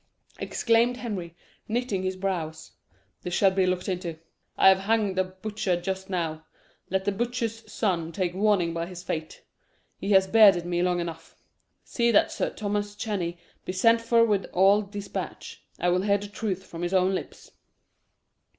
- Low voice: No, high, 190 Hz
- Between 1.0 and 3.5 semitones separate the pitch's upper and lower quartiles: Yes, average, 3.0 semitones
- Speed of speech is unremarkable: Yes, average, 170 wpm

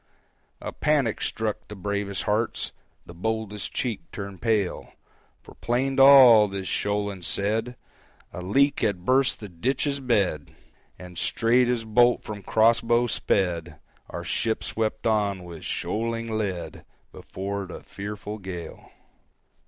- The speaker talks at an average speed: No, slow, 130 wpm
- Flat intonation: No, average, 3.2 semitones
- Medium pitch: No, low, 105 Hz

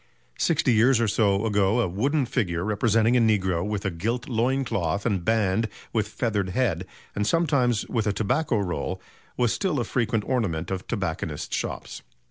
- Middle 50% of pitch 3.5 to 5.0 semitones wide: Yes, average, 4.1 semitones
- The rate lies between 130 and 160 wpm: No, average, 170 wpm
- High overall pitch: No, low, 110 Hz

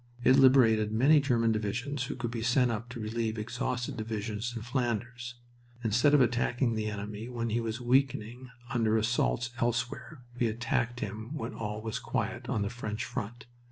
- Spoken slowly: No, average, 170 wpm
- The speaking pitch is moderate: No, low, 115 Hz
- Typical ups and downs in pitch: No, narrow, 2.2 semitones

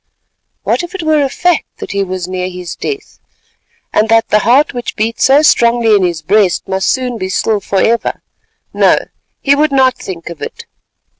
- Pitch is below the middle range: No, high, 225 Hz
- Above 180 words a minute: Yes, average, 190 wpm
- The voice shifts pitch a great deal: Yes, wide, 6.3 semitones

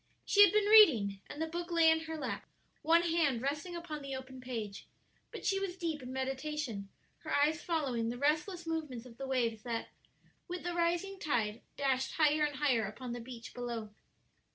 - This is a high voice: Yes, very high, 290 Hz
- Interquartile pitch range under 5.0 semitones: No, average, 5.3 semitones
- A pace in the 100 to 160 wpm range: No, average, 190 wpm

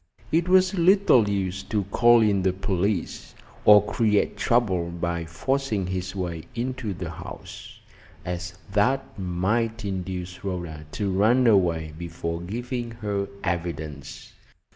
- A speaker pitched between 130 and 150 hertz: No, very low, 95 Hz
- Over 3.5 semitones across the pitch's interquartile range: Yes, average, 4.8 semitones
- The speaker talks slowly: Yes, slow, 125 wpm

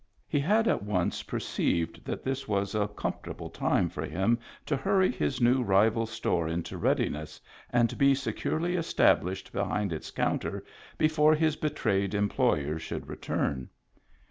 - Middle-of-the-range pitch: No, low, 110 Hz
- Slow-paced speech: No, average, 145 wpm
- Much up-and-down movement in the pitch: Yes, wide, 7.5 semitones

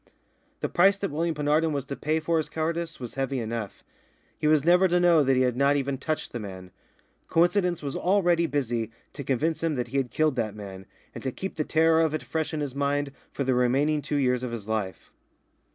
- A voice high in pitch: No, medium, 145 Hz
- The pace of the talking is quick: Yes, fast, 225 wpm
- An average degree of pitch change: Yes, average, 4.4 semitones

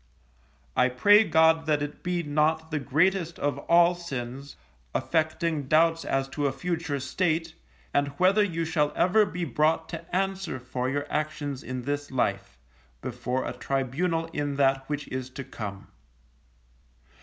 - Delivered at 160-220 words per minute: No, average, 150 wpm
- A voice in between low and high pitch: Yes, medium, 150 Hz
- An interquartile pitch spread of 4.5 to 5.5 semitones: No, average, 3.7 semitones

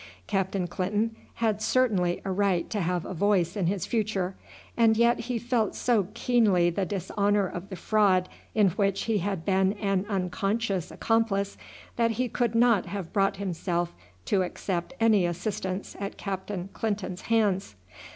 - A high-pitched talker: Yes, high, 200 Hz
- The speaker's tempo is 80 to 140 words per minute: No, average, 155 wpm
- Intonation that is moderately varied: Yes, average, 3.0 semitones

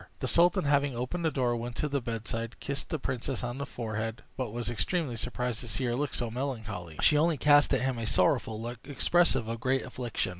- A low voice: Yes, low, 125 Hz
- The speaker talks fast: Yes, fast, 220 wpm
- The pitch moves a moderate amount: Yes, average, 3.6 semitones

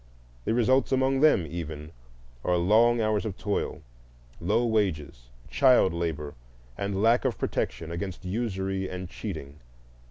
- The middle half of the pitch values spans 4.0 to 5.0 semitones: No, wide, 5.4 semitones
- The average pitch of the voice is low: Yes, very low, 95 Hz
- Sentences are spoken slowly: Yes, slow, 130 wpm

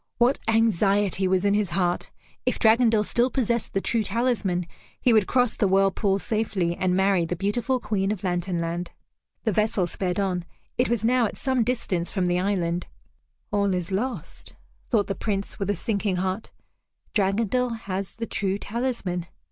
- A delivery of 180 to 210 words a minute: No, average, 170 wpm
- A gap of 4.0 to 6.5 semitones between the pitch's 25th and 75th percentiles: No, average, 3.4 semitones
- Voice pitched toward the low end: No, high, 200 Hz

